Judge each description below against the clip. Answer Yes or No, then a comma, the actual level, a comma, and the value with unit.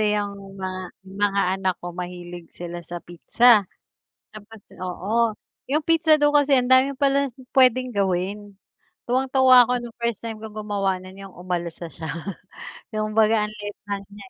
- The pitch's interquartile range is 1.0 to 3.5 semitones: No, average, 4.8 semitones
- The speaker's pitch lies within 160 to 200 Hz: No, high, 210 Hz